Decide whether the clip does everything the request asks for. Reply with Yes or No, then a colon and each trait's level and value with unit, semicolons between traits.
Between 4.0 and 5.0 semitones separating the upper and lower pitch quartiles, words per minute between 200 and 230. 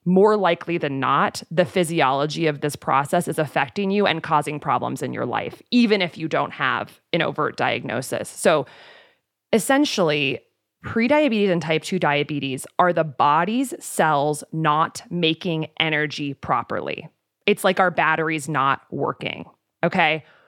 No: average, 4.3 semitones; average, 140 wpm